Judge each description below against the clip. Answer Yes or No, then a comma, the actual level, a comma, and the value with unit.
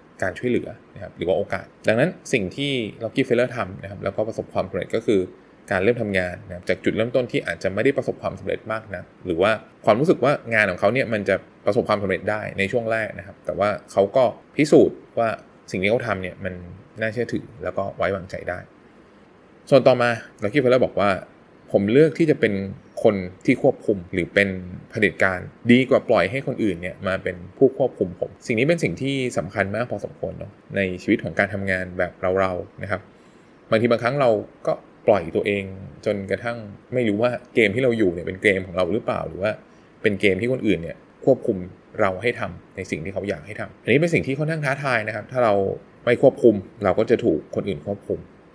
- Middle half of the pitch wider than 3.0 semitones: Yes, average, 4.4 semitones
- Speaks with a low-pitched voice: Yes, low, 105 Hz